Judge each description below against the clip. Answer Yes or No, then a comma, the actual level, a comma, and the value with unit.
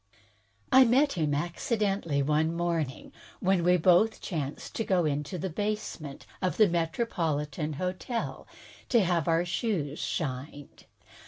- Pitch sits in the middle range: Yes, medium, 170 Hz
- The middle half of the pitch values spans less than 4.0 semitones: No, average, 4.4 semitones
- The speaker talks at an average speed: No, slow, 130 wpm